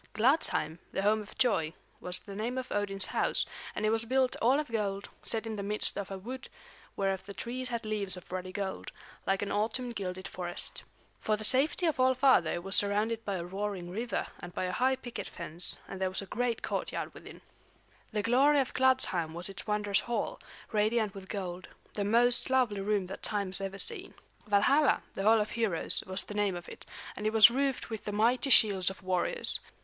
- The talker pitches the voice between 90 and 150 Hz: No, high, 210 Hz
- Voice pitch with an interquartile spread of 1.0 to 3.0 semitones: No, average, 3.8 semitones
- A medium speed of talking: No, fast, 210 wpm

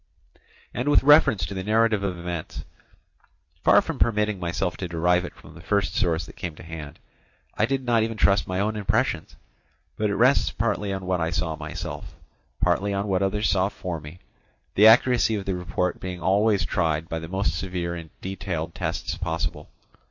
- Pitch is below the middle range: Yes, very low, 95 Hz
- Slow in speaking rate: No, average, 190 wpm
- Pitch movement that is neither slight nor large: Yes, average, 3.6 semitones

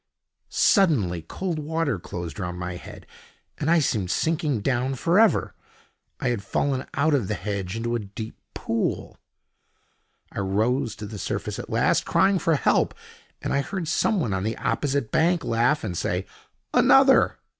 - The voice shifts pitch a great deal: Yes, wide, 7.8 semitones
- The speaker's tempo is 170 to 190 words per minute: No, average, 160 wpm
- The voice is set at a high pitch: No, low, 120 Hz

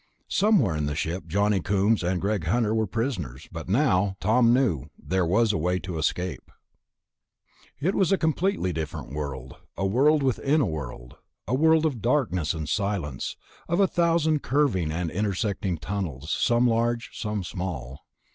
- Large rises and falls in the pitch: Yes, wide, 7.4 semitones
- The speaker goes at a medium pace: Yes, average, 160 wpm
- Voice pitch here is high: No, low, 100 Hz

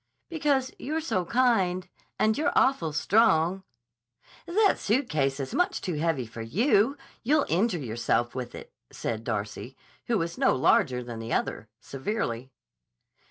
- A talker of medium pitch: Yes, medium, 175 Hz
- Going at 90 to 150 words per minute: Yes, average, 140 wpm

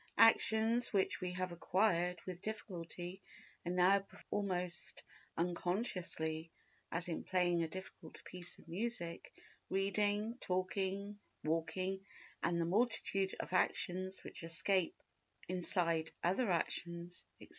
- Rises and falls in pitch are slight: Yes, narrow, 2.3 semitones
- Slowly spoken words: Yes, slow, 120 wpm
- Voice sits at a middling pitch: Yes, medium, 180 Hz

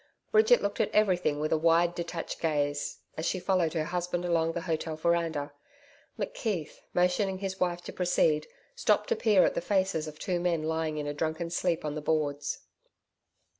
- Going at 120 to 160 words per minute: No, average, 185 wpm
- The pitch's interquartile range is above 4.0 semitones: No, average, 2.7 semitones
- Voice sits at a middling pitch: Yes, medium, 170 Hz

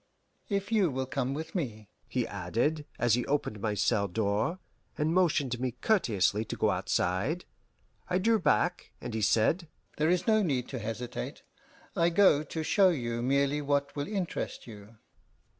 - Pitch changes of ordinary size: No, wide, 7.0 semitones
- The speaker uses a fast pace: No, average, 165 wpm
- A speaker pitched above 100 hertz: Yes, medium, 140 Hz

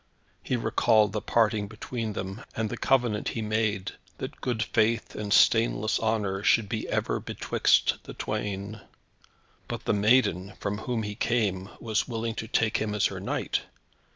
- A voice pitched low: Yes, low, 110 Hz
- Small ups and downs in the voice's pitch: Yes, narrow, 1.7 semitones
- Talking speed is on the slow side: No, average, 160 wpm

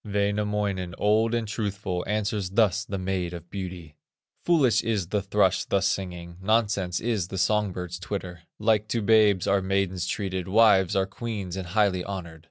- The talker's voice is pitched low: Yes, low, 100 Hz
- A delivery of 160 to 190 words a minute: Yes, average, 170 wpm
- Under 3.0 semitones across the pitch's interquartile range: Yes, narrow, 2.5 semitones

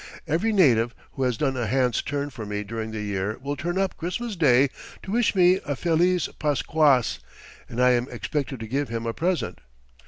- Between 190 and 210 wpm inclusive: Yes, average, 195 wpm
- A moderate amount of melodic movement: No, wide, 6.5 semitones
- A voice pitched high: No, low, 135 Hz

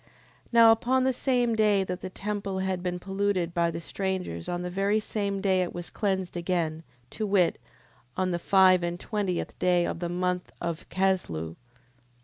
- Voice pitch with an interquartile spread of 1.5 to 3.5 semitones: Yes, narrow, 2.4 semitones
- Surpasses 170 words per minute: Yes, average, 180 wpm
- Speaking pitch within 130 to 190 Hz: Yes, medium, 185 Hz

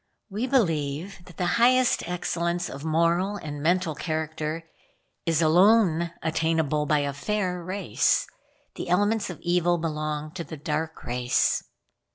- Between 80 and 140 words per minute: Yes, slow, 135 wpm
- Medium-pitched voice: Yes, medium, 165 Hz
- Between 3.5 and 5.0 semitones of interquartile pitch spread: No, average, 3.0 semitones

